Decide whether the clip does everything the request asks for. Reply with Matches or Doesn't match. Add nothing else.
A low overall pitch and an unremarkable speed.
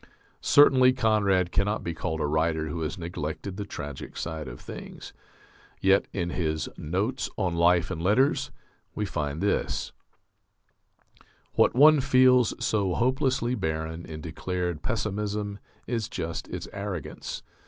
Doesn't match